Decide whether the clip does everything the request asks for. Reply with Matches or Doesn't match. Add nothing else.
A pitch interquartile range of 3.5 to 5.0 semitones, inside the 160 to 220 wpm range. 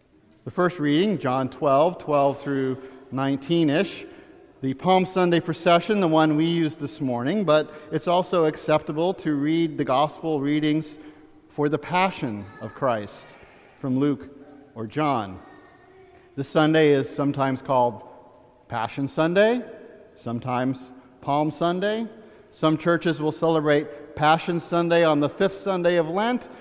Doesn't match